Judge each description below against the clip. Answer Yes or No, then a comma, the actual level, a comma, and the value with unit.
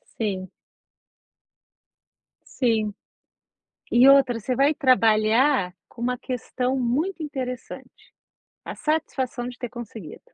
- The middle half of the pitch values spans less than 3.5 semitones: Yes, average, 2.9 semitones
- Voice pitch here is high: Yes, very high, 250 Hz